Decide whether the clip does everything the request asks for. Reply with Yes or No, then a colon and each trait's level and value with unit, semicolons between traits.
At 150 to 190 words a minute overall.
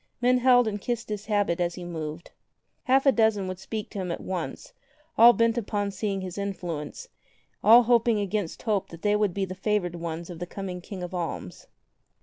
No: average, 200 wpm